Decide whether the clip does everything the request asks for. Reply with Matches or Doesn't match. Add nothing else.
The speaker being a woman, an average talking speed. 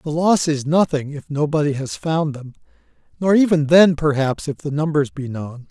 Doesn't match